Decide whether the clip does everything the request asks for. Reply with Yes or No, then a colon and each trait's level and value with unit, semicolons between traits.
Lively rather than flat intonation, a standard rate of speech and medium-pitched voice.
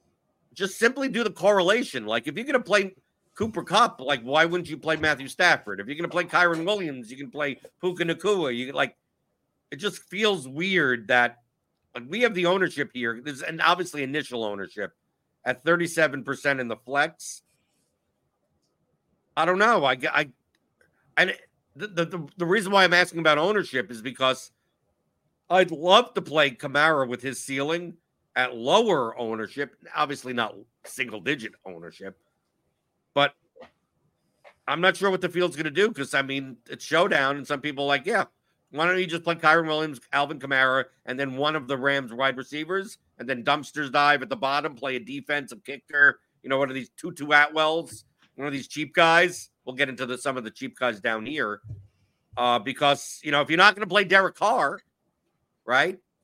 No: average, 4.8 semitones; average, 180 wpm; medium, 145 Hz